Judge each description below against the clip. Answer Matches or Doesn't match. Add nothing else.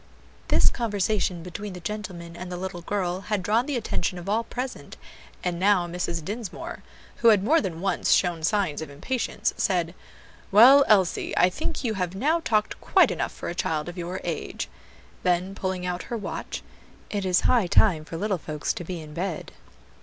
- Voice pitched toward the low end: Doesn't match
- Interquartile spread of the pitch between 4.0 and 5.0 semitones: Doesn't match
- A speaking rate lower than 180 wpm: Doesn't match